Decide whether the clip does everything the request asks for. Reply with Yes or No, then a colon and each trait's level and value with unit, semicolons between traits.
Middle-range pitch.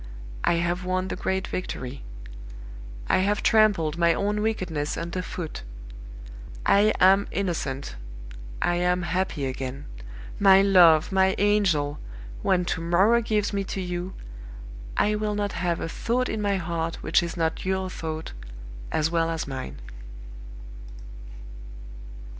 Yes: medium, 180 Hz